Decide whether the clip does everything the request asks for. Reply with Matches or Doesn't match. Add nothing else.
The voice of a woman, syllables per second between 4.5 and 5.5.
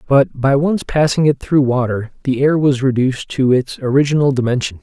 Doesn't match